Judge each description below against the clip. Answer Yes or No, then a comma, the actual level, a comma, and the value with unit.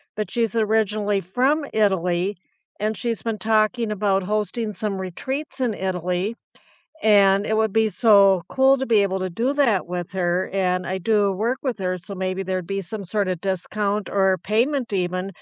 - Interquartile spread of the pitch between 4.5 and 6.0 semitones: No, average, 2.9 semitones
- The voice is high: Yes, high, 200 Hz